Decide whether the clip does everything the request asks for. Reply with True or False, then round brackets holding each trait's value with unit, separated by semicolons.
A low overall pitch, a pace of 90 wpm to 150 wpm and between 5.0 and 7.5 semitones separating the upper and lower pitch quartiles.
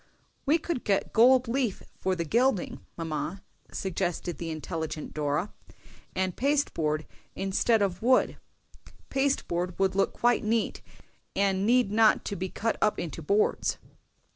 False (195 Hz; 140 wpm; 5.3 semitones)